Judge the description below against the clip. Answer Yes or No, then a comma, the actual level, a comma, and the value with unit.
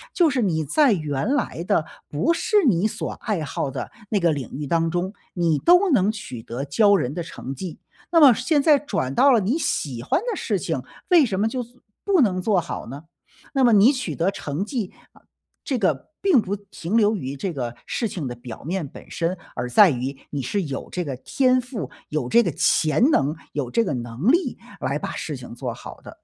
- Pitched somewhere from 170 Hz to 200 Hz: Yes, medium, 185 Hz